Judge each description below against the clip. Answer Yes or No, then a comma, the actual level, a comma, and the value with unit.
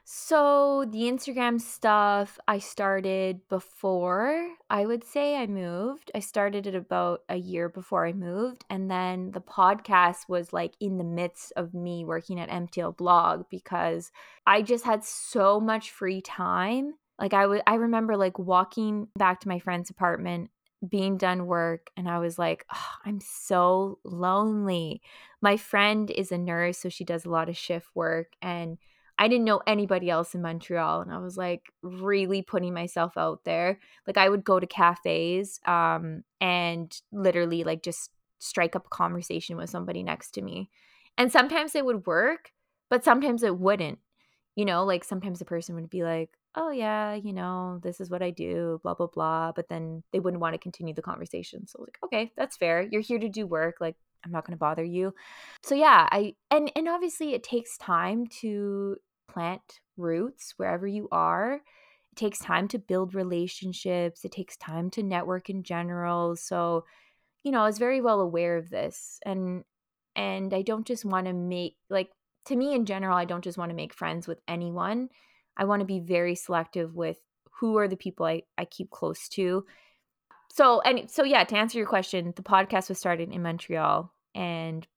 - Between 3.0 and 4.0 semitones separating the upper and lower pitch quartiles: Yes, average, 3.5 semitones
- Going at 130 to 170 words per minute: No, average, 185 wpm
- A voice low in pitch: No, medium, 185 Hz